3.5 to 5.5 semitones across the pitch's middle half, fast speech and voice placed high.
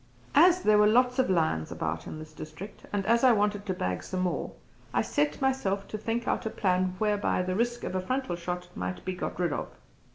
Yes: average, 4.5 semitones; fast, 225 wpm; high, 195 Hz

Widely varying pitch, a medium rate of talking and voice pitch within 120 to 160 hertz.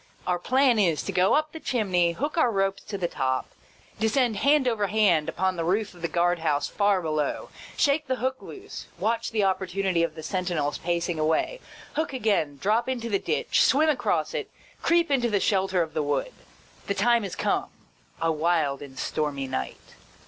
No: wide, 6.3 semitones; average, 190 wpm; high, 195 Hz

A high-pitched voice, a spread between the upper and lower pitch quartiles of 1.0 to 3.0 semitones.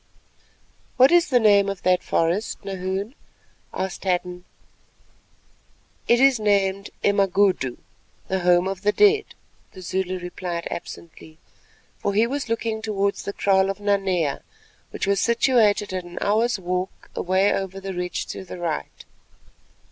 Yes: high, 195 Hz; narrow, 2.4 semitones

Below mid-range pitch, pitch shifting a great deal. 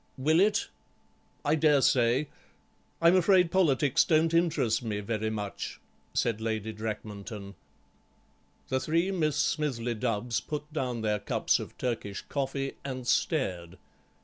Yes: low, 130 Hz; wide, 5.9 semitones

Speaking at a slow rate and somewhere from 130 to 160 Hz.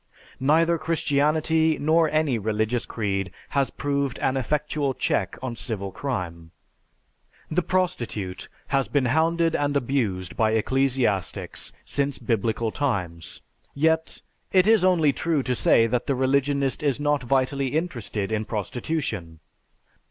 Yes: slow, 125 wpm; low, 135 Hz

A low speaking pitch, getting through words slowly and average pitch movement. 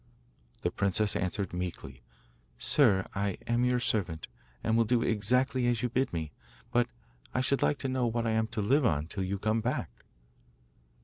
No: low, 110 Hz; average, 180 wpm; average, 4.2 semitones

